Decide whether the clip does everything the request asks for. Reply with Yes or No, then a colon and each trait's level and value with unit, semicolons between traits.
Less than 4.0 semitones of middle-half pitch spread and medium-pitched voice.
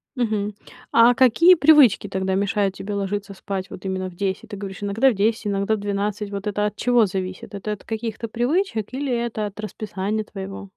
No: narrow, 2.6 semitones; high, 210 Hz